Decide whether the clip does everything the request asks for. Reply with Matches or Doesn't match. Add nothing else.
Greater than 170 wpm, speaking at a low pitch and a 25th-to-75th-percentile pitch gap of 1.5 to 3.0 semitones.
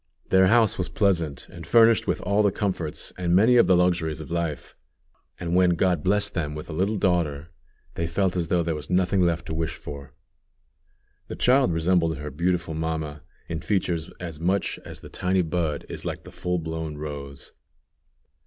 Matches